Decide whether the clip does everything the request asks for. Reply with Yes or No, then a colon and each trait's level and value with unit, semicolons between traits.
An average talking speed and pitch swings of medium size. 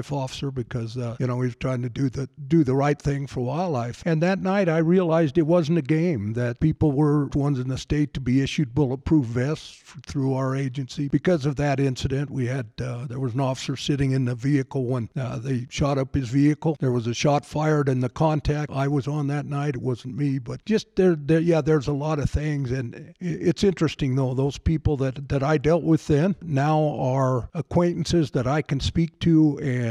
No: fast, 220 wpm; average, 3.0 semitones